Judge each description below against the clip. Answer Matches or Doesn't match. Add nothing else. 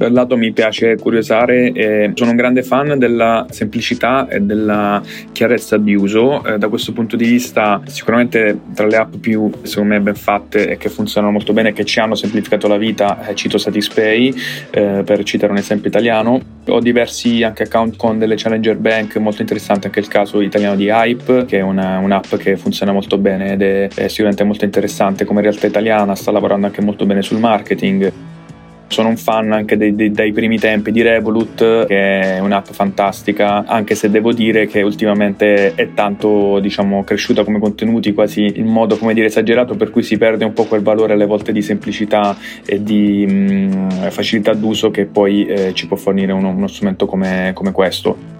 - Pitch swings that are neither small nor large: Doesn't match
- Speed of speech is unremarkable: Doesn't match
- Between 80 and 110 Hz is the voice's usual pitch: Matches